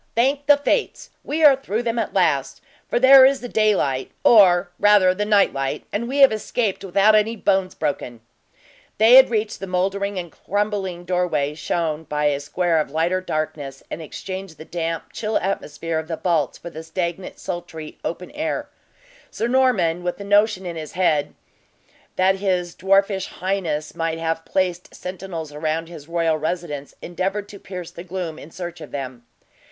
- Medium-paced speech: Yes, average, 170 wpm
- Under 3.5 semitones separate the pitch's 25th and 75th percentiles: No, average, 4.1 semitones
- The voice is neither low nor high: Yes, medium, 180 Hz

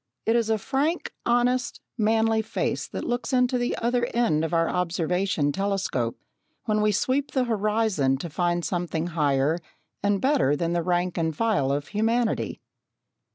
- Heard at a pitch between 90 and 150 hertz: No, high, 200 Hz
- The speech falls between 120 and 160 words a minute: Yes, average, 155 wpm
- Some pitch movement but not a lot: No, wide, 6.0 semitones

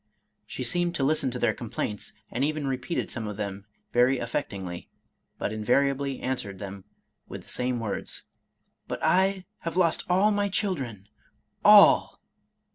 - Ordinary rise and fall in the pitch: No, wide, 7.8 semitones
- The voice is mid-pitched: No, low, 130 Hz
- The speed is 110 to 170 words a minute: Yes, average, 160 wpm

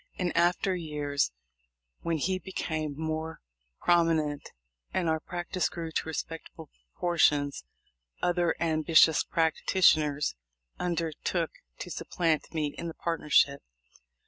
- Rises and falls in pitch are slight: Yes, narrow, 2.1 semitones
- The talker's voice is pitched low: No, medium, 160 Hz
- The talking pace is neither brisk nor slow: No, slow, 110 wpm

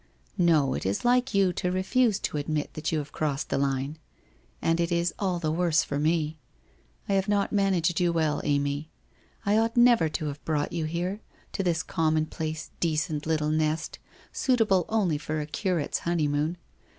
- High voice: No, medium, 160 Hz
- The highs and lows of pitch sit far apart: No, average, 3.5 semitones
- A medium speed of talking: Yes, average, 180 wpm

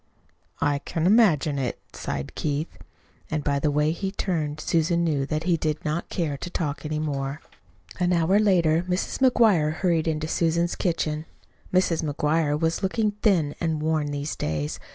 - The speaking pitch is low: No, medium, 160 Hz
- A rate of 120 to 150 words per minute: No, average, 170 wpm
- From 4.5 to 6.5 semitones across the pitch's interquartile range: No, average, 2.7 semitones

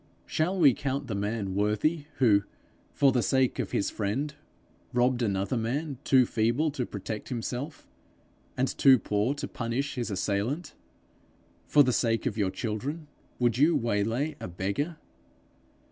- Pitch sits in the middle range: No, low, 125 Hz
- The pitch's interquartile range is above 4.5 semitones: Yes, average, 5.0 semitones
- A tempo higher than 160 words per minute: No, average, 145 wpm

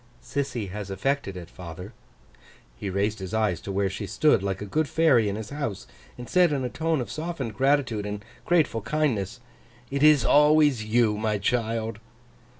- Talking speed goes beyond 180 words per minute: No, average, 175 wpm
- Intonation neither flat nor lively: No, wide, 6.0 semitones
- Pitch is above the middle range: No, low, 115 Hz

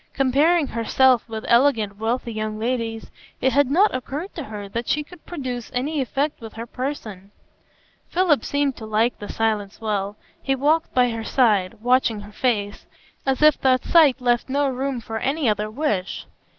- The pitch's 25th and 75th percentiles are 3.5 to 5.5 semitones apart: Yes, average, 4.2 semitones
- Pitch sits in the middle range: No, high, 245 Hz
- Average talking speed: Yes, average, 175 wpm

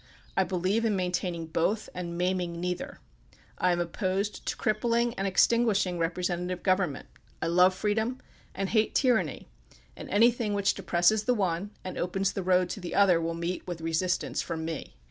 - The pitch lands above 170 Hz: Yes, medium, 185 Hz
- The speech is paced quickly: No, average, 170 wpm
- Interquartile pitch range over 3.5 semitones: No, average, 3.0 semitones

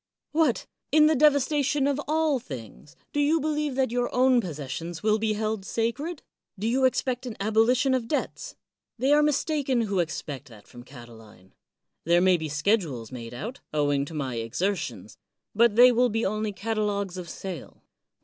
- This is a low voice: No, high, 220 Hz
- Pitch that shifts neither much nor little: No, wide, 8.8 semitones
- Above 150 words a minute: Yes, average, 175 wpm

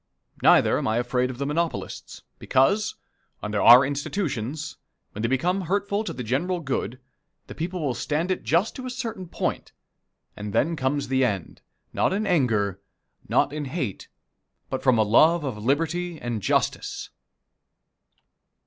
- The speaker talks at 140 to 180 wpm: Yes, average, 155 wpm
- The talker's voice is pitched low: No, medium, 145 Hz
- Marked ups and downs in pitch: Yes, wide, 6.3 semitones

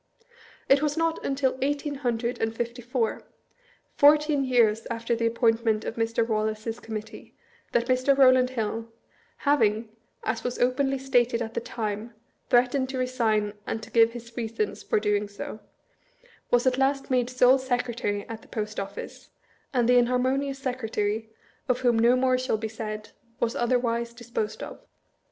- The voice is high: Yes, high, 240 Hz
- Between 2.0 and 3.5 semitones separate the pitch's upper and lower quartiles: Yes, narrow, 2.5 semitones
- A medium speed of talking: Yes, average, 155 wpm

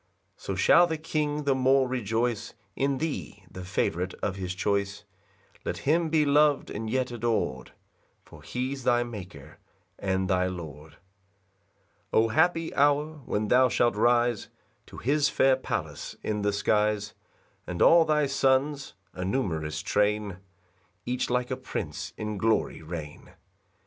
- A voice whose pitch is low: Yes, low, 120 Hz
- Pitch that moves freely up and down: Yes, wide, 5.8 semitones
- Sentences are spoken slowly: No, average, 145 wpm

